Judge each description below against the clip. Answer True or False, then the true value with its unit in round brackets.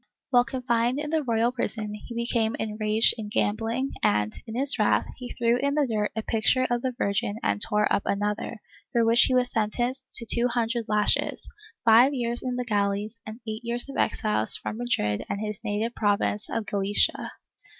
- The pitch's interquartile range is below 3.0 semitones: True (2.6 semitones)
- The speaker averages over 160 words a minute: True (190 wpm)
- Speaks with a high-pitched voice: True (230 Hz)